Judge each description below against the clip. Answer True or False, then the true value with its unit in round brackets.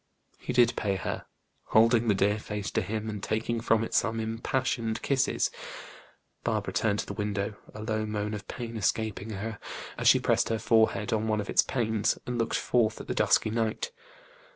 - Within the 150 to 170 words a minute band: False (190 wpm)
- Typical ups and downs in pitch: False (1.5 semitones)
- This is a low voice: True (110 Hz)